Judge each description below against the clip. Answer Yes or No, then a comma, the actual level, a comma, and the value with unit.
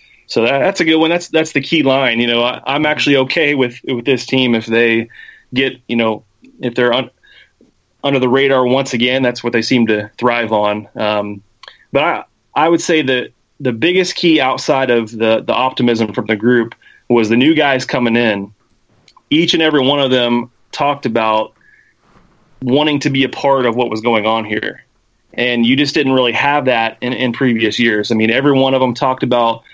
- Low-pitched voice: Yes, low, 125 Hz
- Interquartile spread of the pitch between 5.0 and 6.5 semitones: No, average, 2.9 semitones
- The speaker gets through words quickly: Yes, fast, 210 wpm